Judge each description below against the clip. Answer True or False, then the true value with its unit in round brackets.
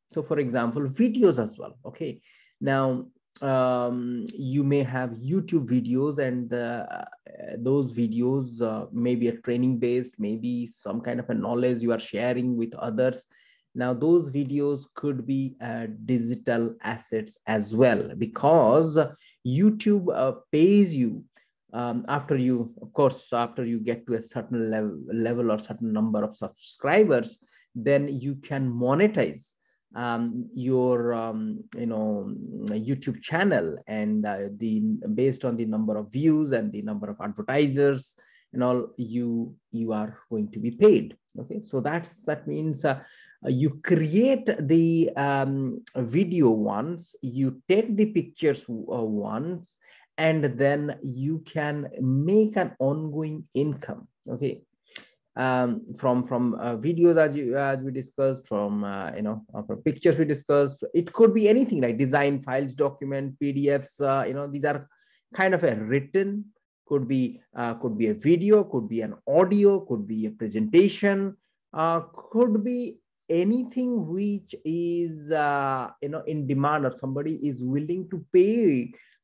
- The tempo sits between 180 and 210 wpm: False (150 wpm)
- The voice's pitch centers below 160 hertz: True (135 Hz)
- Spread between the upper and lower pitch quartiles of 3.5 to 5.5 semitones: True (5.1 semitones)